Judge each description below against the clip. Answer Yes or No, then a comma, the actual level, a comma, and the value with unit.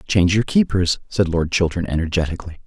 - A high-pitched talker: No, very low, 90 Hz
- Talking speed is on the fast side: No, average, 155 wpm